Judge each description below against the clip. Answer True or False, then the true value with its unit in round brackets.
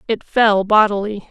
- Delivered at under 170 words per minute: True (140 wpm)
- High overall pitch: True (210 Hz)